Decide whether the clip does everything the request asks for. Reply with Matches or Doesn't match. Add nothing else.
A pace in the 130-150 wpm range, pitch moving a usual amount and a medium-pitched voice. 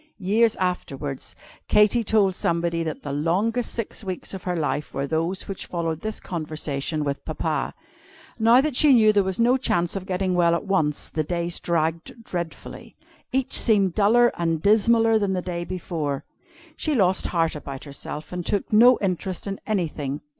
Doesn't match